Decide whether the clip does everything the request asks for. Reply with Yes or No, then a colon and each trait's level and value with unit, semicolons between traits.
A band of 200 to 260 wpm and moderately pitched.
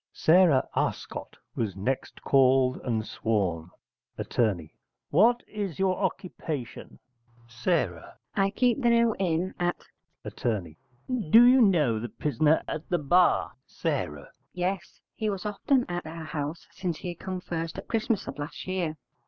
No: average, 140 wpm; medium, 170 Hz